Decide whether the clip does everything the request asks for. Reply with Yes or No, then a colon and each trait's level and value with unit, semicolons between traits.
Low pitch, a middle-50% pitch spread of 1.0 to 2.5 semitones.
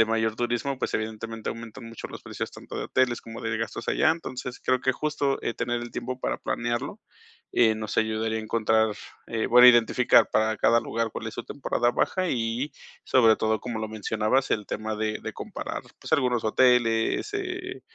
Yes: low, 115 Hz; narrow, 2.2 semitones